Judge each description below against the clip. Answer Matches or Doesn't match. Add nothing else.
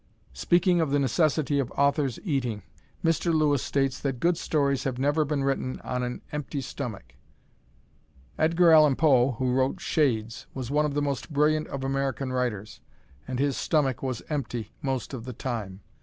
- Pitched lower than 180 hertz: Matches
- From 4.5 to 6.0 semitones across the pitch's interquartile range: Doesn't match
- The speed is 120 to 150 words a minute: Doesn't match